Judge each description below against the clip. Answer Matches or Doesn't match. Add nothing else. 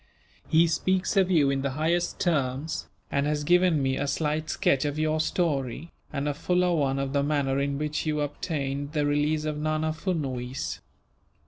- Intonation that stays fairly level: Matches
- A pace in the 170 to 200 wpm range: Matches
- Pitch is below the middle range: Doesn't match